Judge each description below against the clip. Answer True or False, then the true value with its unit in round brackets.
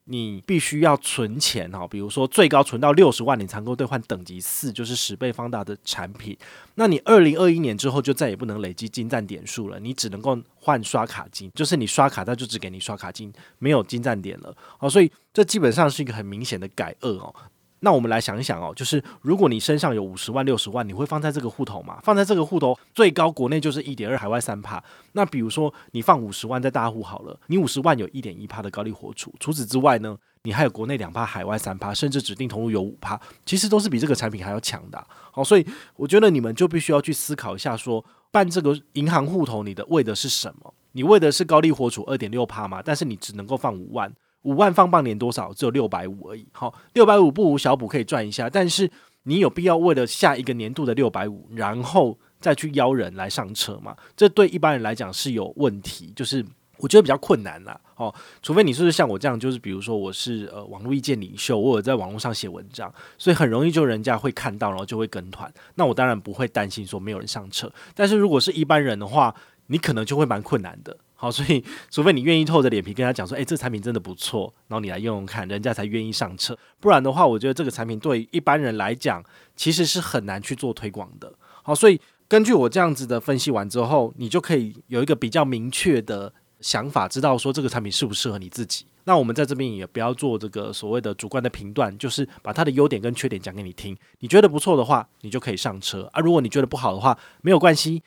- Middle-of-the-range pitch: False (125 Hz)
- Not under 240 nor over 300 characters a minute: False (365 characters per minute)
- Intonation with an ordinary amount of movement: False (5.7 semitones)